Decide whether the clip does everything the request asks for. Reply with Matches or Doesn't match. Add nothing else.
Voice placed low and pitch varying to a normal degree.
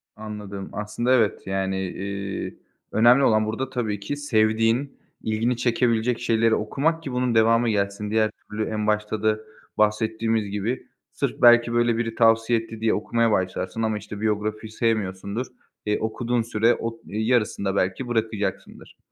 Doesn't match